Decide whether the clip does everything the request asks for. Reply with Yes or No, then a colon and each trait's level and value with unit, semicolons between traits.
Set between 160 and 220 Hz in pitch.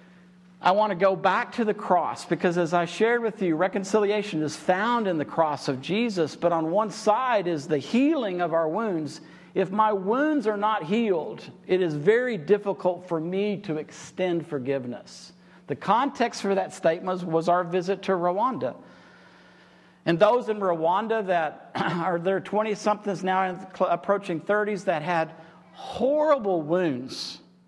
Yes: medium, 185 Hz